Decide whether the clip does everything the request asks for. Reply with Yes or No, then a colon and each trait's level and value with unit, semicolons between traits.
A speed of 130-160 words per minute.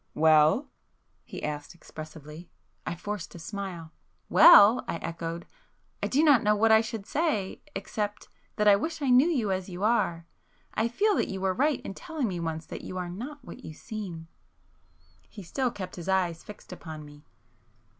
No: average, 170 wpm